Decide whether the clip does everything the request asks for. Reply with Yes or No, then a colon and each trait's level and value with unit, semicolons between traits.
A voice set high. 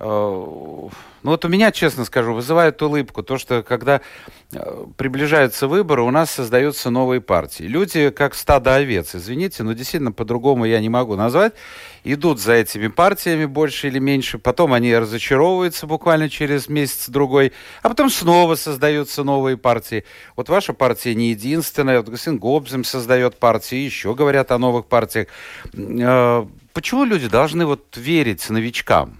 No: low, 135 Hz